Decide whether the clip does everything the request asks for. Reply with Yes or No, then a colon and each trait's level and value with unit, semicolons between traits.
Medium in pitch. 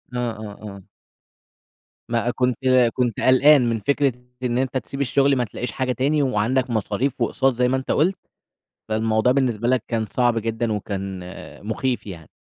No: low, 120 Hz